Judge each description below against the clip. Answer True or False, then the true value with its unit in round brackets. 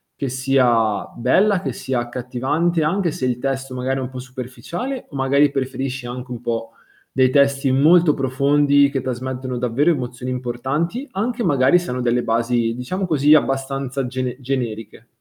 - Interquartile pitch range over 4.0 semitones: False (2.5 semitones)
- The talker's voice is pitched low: True (130 Hz)